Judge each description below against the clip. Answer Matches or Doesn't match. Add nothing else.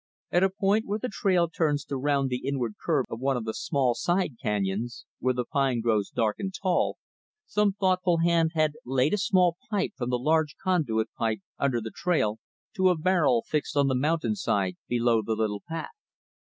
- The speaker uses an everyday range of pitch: Doesn't match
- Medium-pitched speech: Matches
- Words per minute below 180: Doesn't match